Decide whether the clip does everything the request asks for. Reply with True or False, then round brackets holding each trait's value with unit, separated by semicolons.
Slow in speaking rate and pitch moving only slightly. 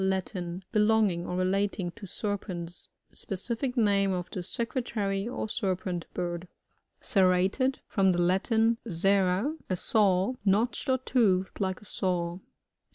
False (130 wpm; 3.3 semitones)